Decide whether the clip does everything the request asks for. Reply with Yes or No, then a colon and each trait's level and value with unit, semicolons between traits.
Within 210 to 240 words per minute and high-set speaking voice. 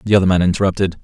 No: fast, 230 wpm; very low, 95 Hz